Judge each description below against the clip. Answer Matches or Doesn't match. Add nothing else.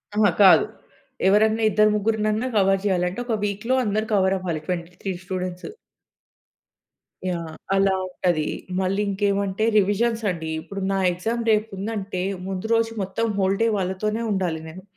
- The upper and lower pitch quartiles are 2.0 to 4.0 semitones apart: Matches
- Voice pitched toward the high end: Matches